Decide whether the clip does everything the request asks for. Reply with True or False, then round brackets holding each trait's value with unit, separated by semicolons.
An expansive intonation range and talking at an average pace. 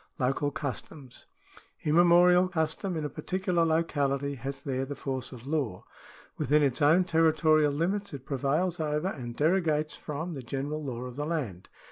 False (3.3 semitones; 160 wpm)